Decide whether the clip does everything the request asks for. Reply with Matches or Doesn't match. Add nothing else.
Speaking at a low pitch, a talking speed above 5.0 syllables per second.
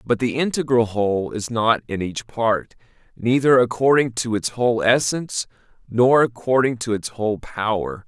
Doesn't match